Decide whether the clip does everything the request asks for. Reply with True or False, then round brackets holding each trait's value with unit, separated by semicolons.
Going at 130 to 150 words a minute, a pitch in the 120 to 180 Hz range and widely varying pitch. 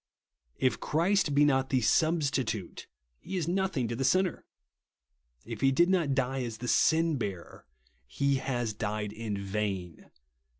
True (140 wpm; 135 Hz; 6.7 semitones)